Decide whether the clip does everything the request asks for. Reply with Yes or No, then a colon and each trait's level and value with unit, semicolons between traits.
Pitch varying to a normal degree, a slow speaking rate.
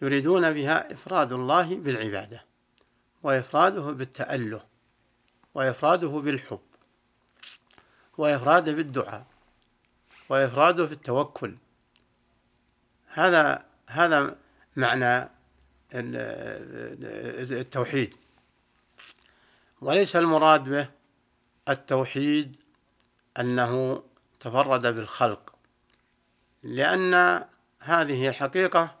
Yes: average, 3.9 semitones; slow, 55 wpm